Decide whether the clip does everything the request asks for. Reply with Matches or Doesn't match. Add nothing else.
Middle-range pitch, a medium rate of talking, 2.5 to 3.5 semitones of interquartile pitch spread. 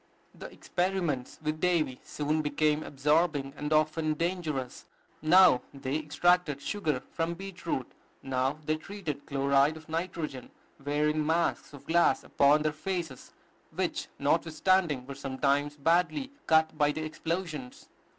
Doesn't match